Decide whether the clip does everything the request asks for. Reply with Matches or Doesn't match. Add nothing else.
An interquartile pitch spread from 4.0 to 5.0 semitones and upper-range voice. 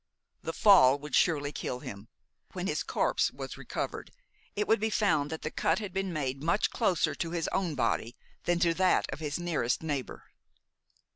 Doesn't match